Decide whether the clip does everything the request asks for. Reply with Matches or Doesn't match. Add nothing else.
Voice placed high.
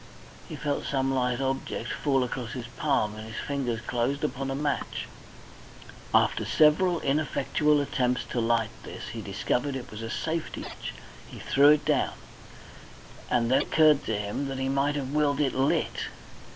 Doesn't match